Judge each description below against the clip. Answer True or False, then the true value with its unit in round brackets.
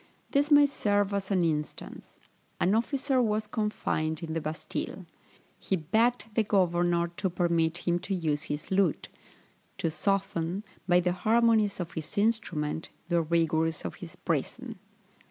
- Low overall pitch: False (180 Hz)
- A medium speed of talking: True (150 wpm)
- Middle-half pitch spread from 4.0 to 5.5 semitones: True (4.5 semitones)